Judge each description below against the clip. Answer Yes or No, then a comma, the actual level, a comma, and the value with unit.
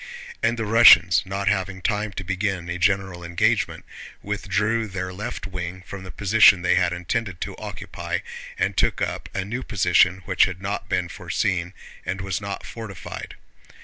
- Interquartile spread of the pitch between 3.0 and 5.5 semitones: No, narrow, 2.4 semitones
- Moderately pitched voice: No, very low, 95 Hz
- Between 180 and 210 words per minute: No, average, 165 wpm